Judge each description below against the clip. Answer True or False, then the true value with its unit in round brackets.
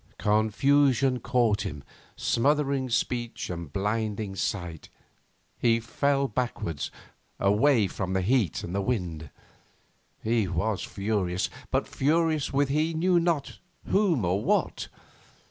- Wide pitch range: True (6.2 semitones)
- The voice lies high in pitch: False (115 Hz)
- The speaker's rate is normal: False (110 wpm)